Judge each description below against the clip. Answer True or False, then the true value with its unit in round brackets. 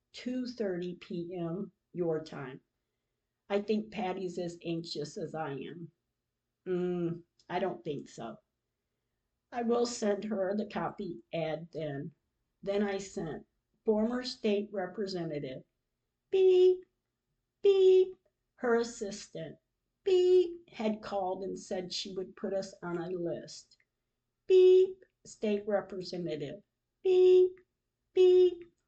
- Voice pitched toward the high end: True (200 Hz)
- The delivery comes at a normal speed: False (110 wpm)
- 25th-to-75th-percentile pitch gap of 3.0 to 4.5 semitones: False (5.6 semitones)